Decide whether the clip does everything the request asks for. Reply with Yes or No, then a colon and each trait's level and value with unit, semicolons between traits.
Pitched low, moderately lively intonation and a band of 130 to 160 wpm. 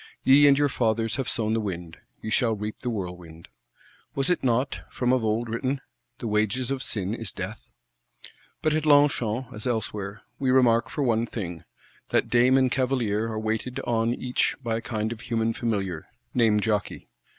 No: low, 115 Hz; average, 3.1 semitones; average, 180 wpm